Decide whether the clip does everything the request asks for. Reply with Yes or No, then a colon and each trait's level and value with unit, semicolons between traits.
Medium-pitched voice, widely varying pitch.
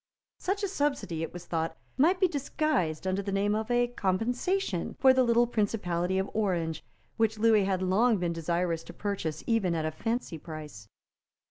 No: high, 200 Hz; wide, 6.1 semitones